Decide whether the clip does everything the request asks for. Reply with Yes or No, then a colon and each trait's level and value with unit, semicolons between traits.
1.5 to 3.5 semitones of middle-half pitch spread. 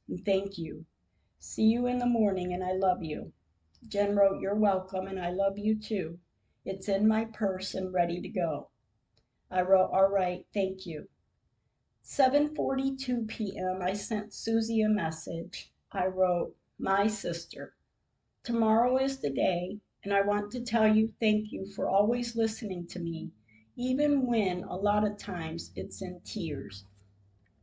No: average, 3.9 semitones